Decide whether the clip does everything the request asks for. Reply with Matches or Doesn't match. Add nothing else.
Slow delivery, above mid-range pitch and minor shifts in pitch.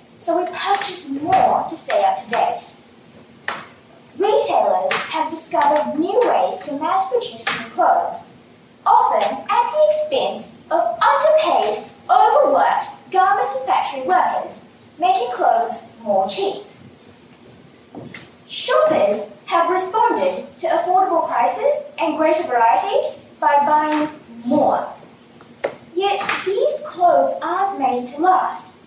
Doesn't match